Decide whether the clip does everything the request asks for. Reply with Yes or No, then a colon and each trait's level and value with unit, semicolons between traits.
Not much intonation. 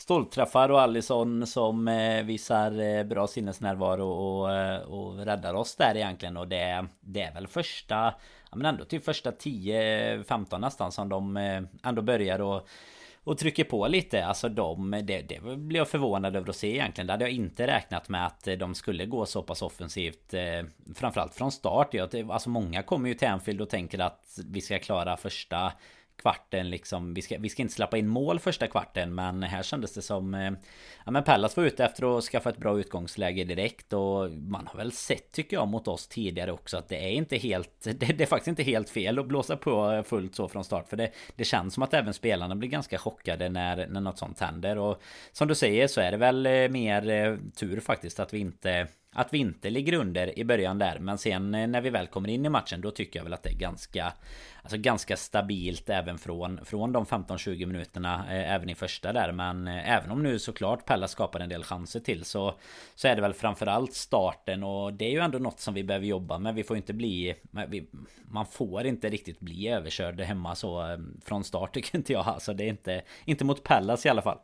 No: average, 3.9 semitones